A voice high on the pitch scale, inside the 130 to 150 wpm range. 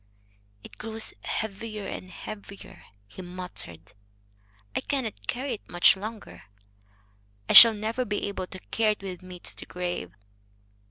Yes: high, 200 Hz; average, 145 wpm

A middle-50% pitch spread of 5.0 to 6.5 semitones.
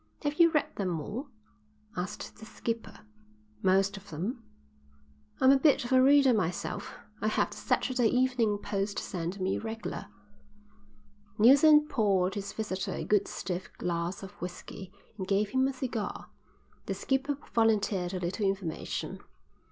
Yes: average, 5.3 semitones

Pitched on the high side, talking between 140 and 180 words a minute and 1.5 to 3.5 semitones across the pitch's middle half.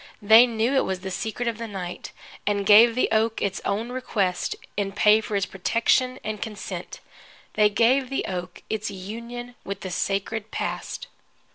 Yes: high, 215 Hz; average, 170 wpm; average, 2.9 semitones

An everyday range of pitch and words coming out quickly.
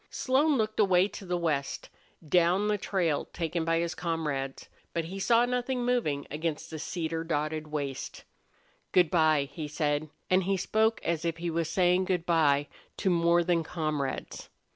No: average, 3.4 semitones; average, 165 wpm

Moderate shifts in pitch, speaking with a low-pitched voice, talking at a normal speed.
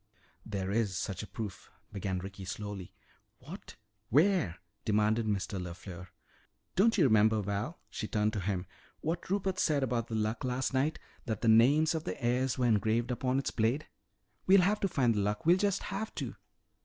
No: wide, 6.5 semitones; low, 115 Hz; average, 180 wpm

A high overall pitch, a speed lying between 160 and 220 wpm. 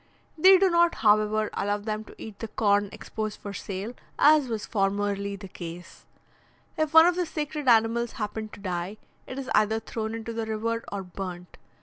Yes: high, 215 Hz; average, 185 wpm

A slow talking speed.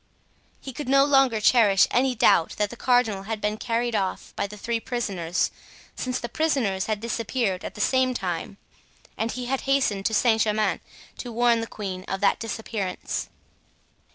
No: average, 175 wpm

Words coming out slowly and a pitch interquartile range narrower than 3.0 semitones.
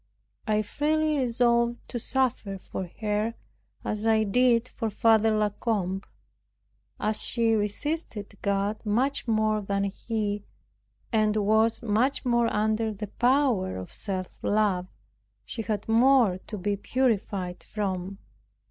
Yes: slow, 125 wpm; narrow, 2.6 semitones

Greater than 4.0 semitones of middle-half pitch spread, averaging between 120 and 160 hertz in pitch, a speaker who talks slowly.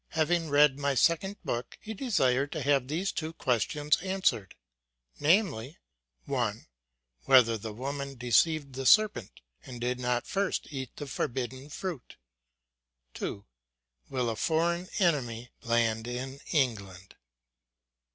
Yes: average, 4.8 semitones; low, 135 Hz; slow, 125 wpm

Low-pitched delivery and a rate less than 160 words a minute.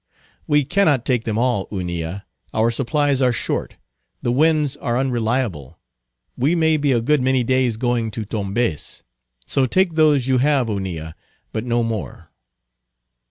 Yes: low, 125 Hz; average, 150 wpm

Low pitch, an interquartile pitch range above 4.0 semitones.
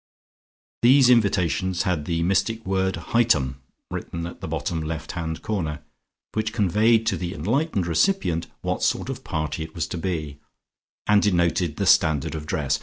Yes: very low, 90 Hz; average, 5.1 semitones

